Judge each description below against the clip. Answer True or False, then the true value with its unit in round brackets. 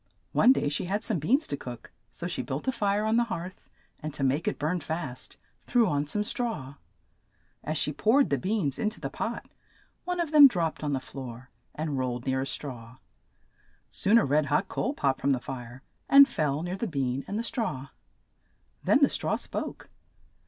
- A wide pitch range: True (8.1 semitones)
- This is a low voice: False (155 Hz)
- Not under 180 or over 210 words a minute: True (200 wpm)